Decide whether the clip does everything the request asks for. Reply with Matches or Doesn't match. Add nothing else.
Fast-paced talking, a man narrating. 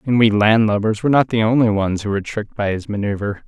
Matches